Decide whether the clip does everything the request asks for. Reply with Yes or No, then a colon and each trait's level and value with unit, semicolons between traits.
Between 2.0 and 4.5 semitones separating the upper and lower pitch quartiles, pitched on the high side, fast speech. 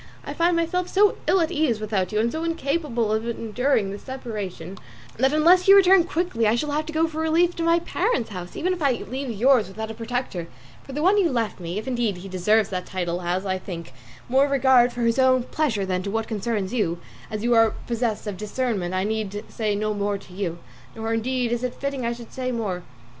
No: wide, 5.5 semitones; high, 235 Hz; fast, 230 wpm